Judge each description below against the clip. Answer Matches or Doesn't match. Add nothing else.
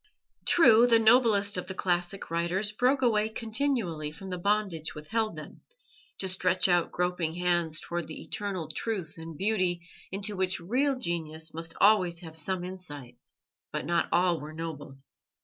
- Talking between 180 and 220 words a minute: Doesn't match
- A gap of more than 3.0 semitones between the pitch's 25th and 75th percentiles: Matches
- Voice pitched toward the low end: Doesn't match